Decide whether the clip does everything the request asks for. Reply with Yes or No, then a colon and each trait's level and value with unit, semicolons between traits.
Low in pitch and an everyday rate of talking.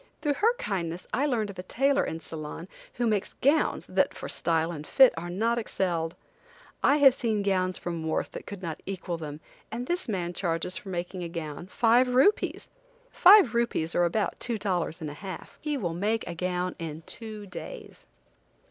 No: high, 190 Hz; average, 190 wpm